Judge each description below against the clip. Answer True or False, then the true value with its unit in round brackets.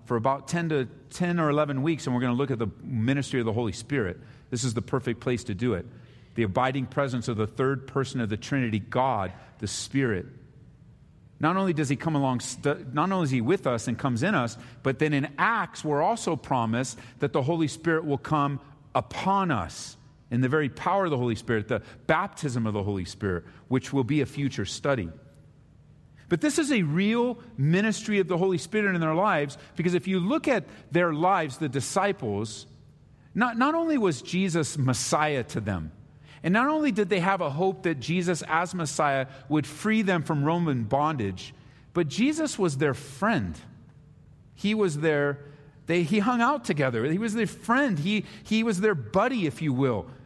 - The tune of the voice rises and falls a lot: True (5.8 semitones)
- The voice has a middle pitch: True (145 Hz)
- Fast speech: False (195 wpm)